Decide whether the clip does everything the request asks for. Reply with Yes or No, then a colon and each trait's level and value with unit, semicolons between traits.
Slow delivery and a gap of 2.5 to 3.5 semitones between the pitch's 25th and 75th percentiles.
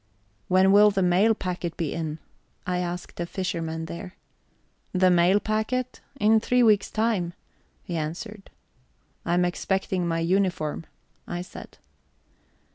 Yes: slow, 130 wpm; average, 3.1 semitones